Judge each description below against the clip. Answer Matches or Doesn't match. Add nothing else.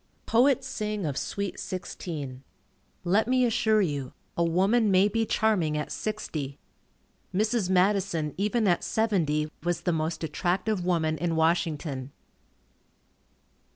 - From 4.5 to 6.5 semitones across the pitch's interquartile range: Matches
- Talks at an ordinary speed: Doesn't match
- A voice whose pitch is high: Doesn't match